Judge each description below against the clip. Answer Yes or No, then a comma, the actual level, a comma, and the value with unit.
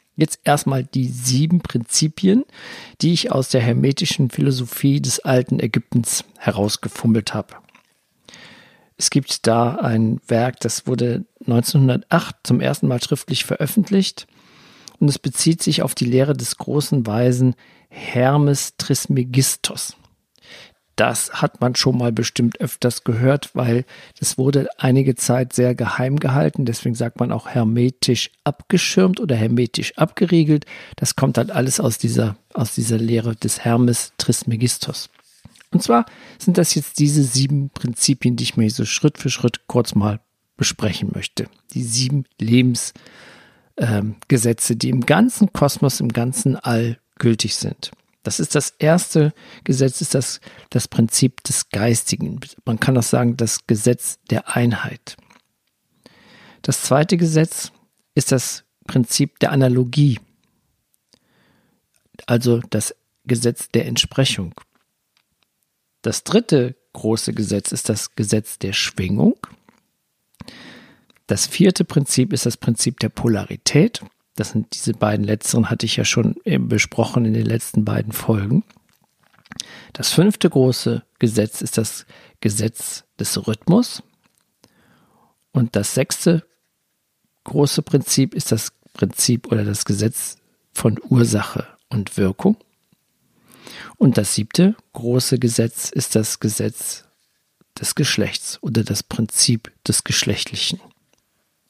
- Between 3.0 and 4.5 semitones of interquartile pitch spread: Yes, average, 3.8 semitones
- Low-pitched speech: Yes, low, 125 Hz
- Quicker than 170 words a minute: No, slow, 125 wpm